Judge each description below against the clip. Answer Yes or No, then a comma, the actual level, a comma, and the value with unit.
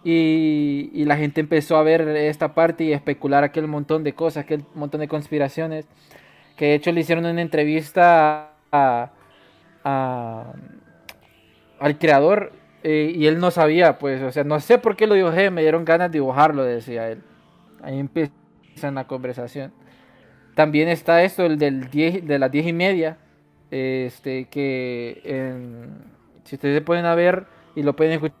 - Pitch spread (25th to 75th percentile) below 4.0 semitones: Yes, average, 2.9 semitones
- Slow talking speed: No, average, 165 wpm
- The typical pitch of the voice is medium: Yes, medium, 150 Hz